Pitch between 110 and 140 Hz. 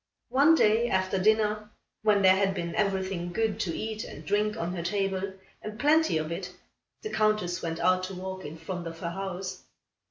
No: high, 190 Hz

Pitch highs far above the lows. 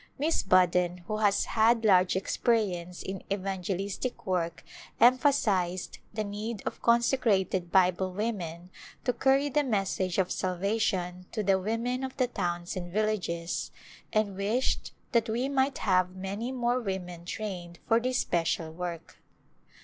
No: average, 4.4 semitones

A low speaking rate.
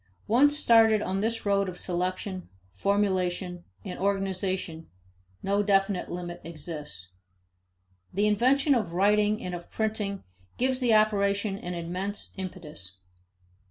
Yes: slow, 120 wpm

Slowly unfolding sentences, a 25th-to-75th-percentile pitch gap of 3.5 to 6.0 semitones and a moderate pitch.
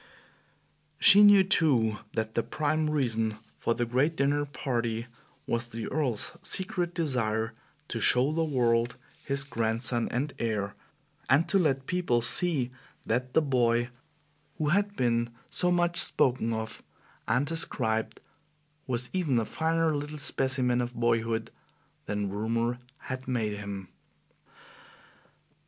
No: slow, 130 wpm; average, 4.8 semitones; low, 125 Hz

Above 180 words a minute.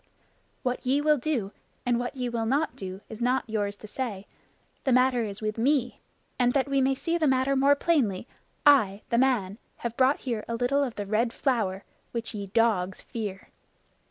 Yes: average, 190 wpm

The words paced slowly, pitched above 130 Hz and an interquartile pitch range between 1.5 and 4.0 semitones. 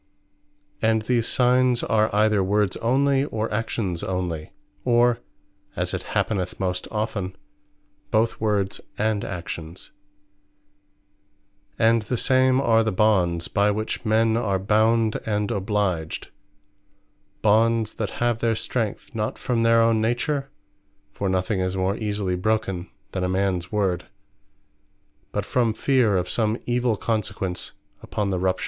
No: slow, 130 wpm; low, 110 Hz; average, 3.3 semitones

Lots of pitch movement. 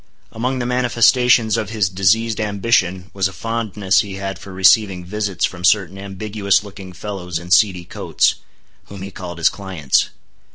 No: average, 2.7 semitones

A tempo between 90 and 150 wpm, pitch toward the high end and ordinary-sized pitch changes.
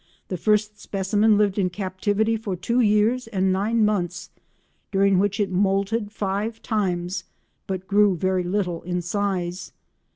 No: average, 140 wpm; high, 200 Hz; narrow, 2.2 semitones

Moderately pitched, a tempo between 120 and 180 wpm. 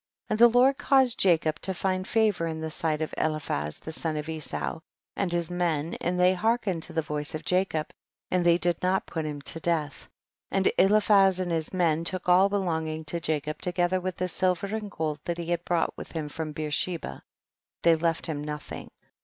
No: medium, 170 Hz; fast, 205 wpm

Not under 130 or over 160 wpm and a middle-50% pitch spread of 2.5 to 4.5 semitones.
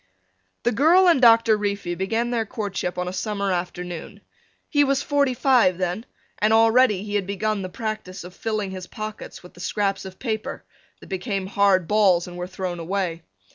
No: average, 180 wpm; average, 3.5 semitones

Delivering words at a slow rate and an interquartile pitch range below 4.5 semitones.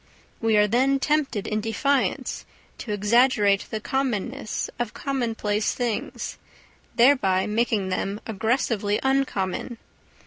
Yes: slow, 105 wpm; average, 3.9 semitones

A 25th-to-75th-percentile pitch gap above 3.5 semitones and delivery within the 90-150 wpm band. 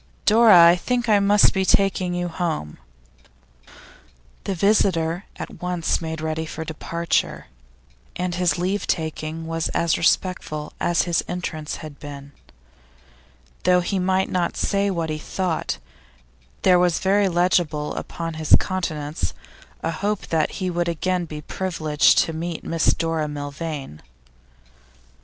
No: narrow, 2.6 semitones; slow, 135 wpm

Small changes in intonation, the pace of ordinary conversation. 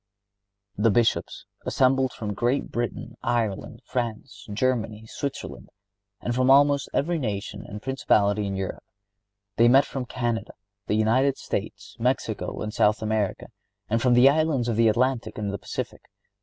No: average, 3.4 semitones; average, 145 wpm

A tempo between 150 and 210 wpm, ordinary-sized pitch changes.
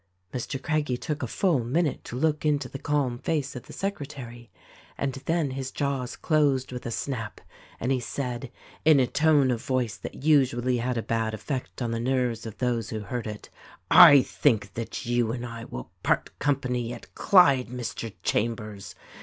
Yes: average, 185 wpm; average, 3.4 semitones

